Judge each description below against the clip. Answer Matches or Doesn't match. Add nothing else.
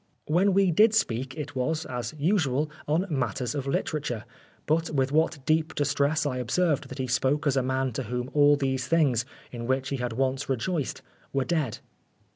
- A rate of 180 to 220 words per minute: Matches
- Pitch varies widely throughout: Doesn't match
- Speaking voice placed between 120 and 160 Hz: Matches